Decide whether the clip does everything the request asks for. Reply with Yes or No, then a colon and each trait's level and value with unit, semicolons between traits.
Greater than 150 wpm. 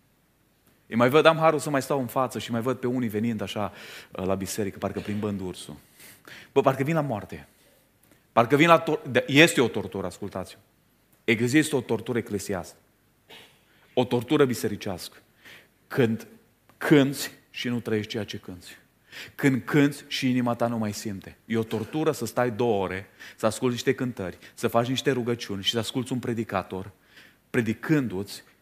Yes: fast, 170 wpm